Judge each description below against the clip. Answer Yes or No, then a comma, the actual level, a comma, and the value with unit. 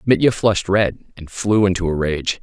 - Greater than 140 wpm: Yes, average, 200 wpm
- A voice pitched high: No, very low, 95 Hz